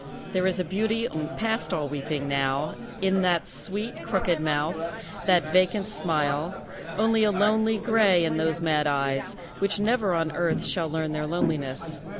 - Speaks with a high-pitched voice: No, medium, 175 Hz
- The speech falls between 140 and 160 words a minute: Yes, average, 155 wpm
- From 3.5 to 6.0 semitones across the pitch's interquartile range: Yes, average, 5.0 semitones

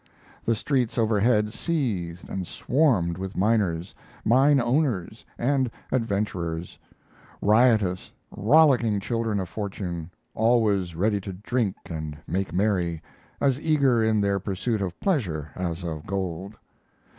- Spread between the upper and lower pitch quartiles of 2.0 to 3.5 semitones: No, average, 4.8 semitones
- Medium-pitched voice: No, low, 105 Hz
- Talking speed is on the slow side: Yes, slow, 120 wpm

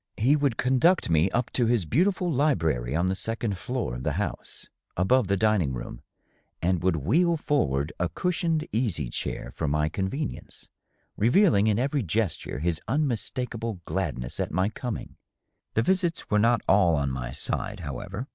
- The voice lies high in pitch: No, low, 110 Hz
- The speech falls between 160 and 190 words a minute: Yes, average, 170 wpm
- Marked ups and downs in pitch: Yes, wide, 7.9 semitones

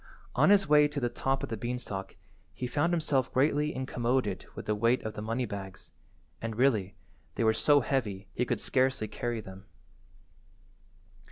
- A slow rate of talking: No, average, 170 wpm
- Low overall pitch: Yes, low, 120 Hz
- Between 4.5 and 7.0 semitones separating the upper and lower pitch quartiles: No, average, 4.1 semitones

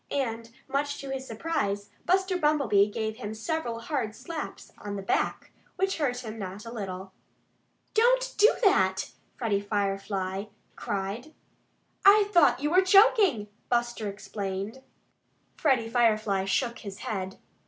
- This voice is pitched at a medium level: No, high, 230 Hz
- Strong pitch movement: Yes, wide, 6.7 semitones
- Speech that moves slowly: Yes, slow, 130 wpm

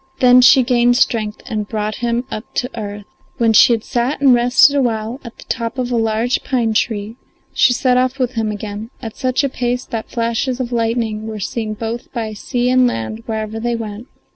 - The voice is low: No, high, 235 Hz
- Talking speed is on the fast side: Yes, fast, 210 wpm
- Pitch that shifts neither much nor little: No, narrow, 2.2 semitones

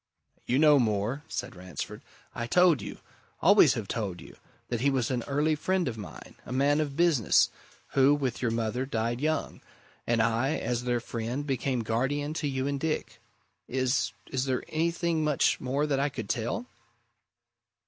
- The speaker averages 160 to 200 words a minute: Yes, average, 170 wpm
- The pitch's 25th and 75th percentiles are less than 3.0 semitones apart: No, average, 3.8 semitones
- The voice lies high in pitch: No, low, 130 Hz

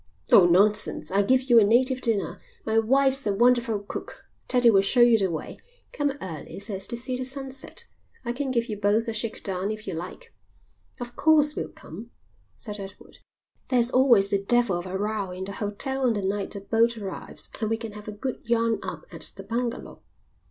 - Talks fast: Yes, fast, 210 wpm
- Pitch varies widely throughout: No, average, 3.8 semitones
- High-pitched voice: Yes, high, 225 Hz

